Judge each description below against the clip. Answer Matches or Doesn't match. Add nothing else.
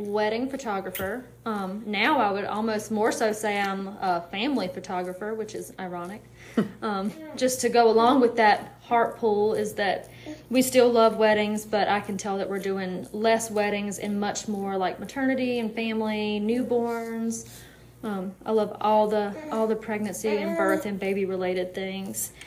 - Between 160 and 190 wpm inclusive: Matches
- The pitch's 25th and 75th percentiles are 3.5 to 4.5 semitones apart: Doesn't match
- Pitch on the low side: Doesn't match